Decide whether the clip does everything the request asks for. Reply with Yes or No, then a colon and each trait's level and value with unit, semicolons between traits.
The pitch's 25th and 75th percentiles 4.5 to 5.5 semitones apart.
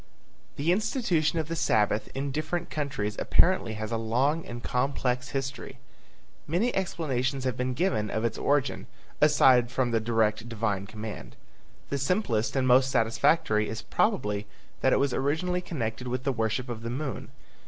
Yes: average, 5.0 semitones